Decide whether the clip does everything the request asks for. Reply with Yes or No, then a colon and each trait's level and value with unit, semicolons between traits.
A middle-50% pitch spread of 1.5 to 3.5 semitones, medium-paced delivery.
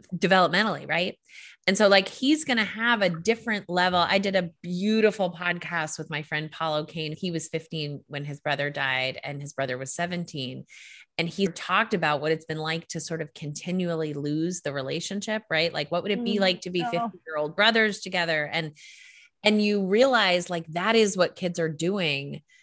No: average, 4.1 semitones; average, 195 wpm